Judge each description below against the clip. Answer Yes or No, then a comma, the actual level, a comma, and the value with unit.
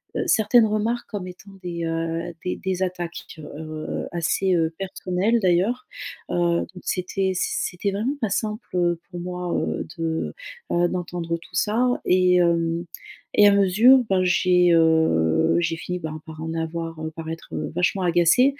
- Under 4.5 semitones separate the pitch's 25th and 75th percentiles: Yes, average, 2.8 semitones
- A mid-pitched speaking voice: Yes, medium, 180 Hz